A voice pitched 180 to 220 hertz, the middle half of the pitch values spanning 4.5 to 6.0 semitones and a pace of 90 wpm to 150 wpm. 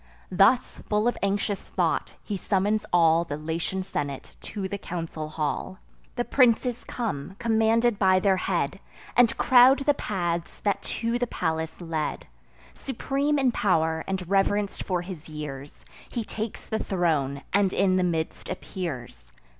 Yes: high, 190 Hz; average, 5.3 semitones; average, 145 wpm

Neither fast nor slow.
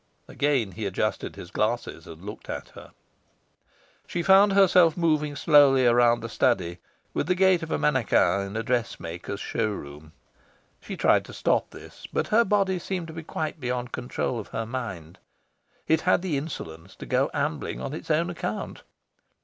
Yes: average, 175 wpm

